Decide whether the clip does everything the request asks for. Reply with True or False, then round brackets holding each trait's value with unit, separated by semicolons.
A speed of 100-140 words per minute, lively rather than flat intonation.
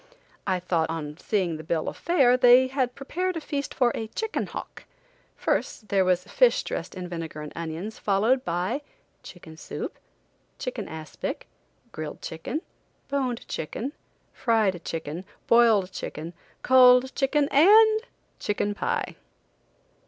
True (135 wpm; 7.9 semitones)